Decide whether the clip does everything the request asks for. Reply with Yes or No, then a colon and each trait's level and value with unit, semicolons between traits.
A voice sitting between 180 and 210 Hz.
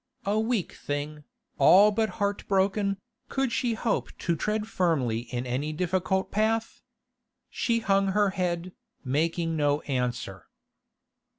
Yes: medium, 185 Hz